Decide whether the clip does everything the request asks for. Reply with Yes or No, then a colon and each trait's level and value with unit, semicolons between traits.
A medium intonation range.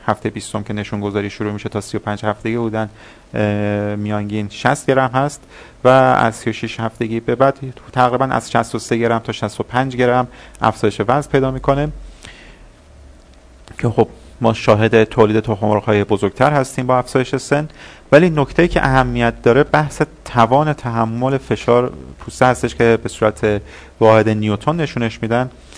Yes: average, 3.5 semitones